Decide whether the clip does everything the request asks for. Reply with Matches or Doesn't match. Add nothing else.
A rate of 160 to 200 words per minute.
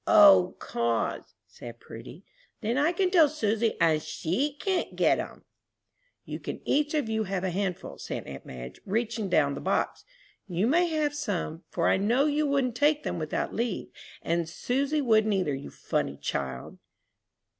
Matches